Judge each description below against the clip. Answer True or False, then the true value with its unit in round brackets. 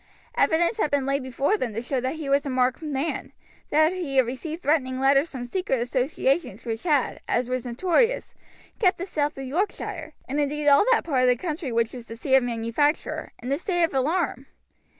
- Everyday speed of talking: False (210 wpm)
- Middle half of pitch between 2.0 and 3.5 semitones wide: False (4.0 semitones)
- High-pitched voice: True (275 Hz)